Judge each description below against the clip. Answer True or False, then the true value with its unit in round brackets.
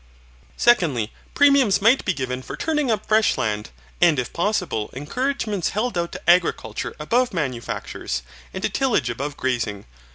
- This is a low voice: False (175 Hz)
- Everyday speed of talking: True (150 wpm)